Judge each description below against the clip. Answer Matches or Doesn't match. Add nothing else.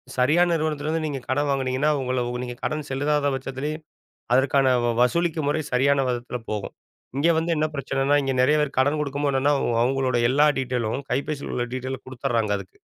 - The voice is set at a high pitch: Doesn't match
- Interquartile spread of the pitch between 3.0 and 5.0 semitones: Doesn't match